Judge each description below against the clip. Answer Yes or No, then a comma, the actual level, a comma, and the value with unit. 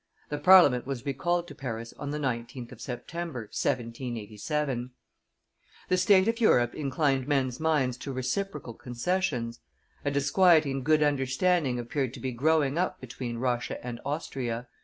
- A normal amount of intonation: Yes, average, 4.2 semitones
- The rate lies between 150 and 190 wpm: No, average, 140 wpm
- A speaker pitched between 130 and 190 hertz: Yes, low, 135 Hz